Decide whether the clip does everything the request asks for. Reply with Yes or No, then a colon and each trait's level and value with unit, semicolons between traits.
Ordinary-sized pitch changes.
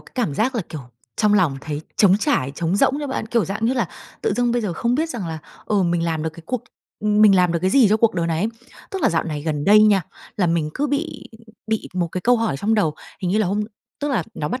No: wide, 5.8 semitones